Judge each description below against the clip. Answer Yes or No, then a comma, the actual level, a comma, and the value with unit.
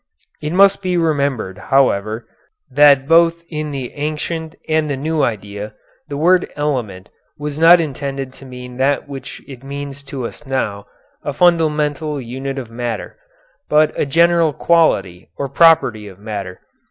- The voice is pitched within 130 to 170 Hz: Yes, medium, 140 Hz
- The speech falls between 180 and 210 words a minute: No, average, 150 wpm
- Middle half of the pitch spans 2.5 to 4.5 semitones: Yes, average, 4.1 semitones